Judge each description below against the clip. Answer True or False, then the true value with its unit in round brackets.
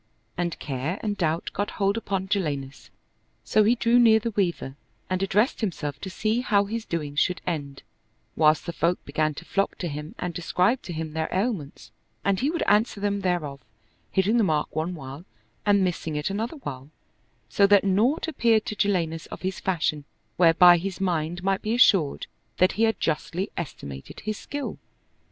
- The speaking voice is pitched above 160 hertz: True (185 Hz)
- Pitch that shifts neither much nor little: True (4.8 semitones)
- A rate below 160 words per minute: False (180 wpm)